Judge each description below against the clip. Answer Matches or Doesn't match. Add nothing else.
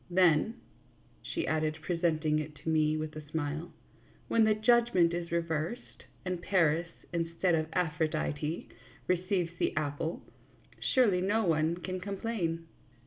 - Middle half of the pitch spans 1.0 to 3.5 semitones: Matches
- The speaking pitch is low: Doesn't match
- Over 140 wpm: Doesn't match